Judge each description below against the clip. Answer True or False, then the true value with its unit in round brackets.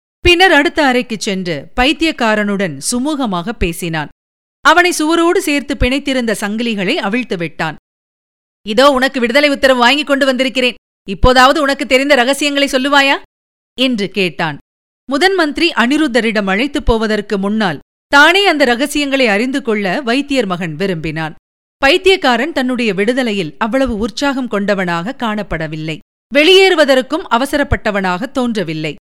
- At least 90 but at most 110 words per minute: True (105 wpm)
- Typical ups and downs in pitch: False (5.9 semitones)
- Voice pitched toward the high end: True (250 Hz)